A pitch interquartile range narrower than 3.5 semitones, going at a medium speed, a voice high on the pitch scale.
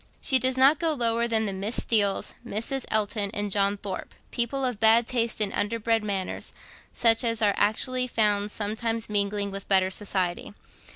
Yes: narrow, 2.5 semitones; average, 170 wpm; high, 220 Hz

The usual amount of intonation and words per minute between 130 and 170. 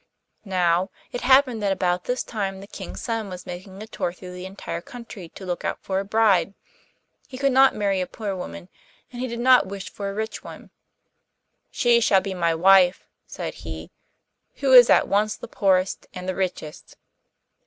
No: average, 3.7 semitones; average, 190 wpm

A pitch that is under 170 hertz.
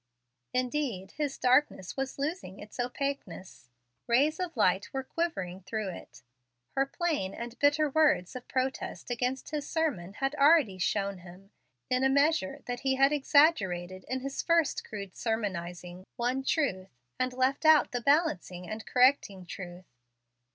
No: very high, 250 Hz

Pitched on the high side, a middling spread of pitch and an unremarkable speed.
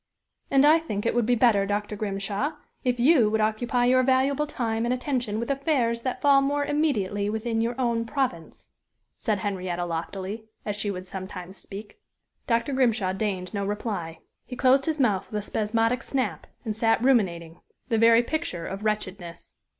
Yes: high, 225 Hz; average, 4.2 semitones; average, 175 wpm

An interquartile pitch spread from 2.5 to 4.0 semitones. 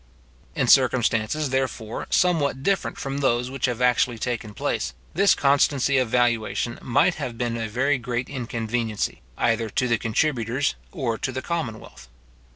Yes: average, 2.9 semitones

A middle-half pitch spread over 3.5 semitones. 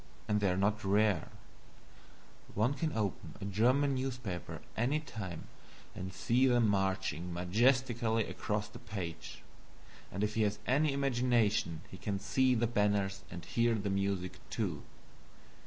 Yes: average, 3.9 semitones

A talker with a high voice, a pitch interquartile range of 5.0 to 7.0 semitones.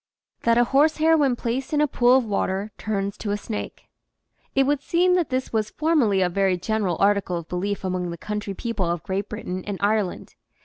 Yes: high, 210 Hz; average, 5.3 semitones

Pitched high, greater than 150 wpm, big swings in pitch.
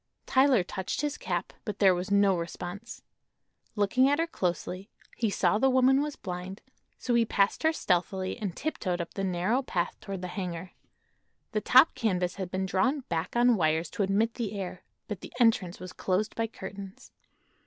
No: high, 195 Hz; average, 180 wpm; average, 4.6 semitones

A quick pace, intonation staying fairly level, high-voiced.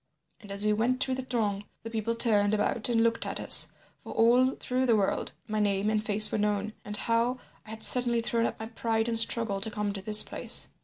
Yes: fast, 225 wpm; narrow, 1.9 semitones; high, 220 Hz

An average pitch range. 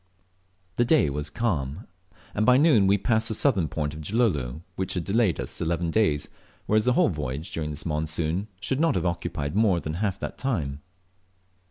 No: wide, 6.4 semitones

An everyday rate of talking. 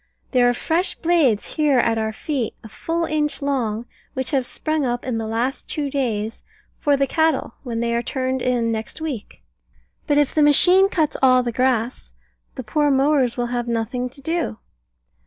Yes: average, 185 wpm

